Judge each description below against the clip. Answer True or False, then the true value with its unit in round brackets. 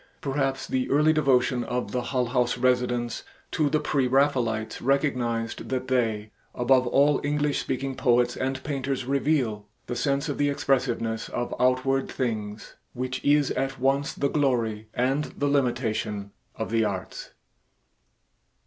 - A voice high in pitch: False (130 Hz)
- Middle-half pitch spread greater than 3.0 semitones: False (2.4 semitones)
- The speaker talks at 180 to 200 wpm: False (140 wpm)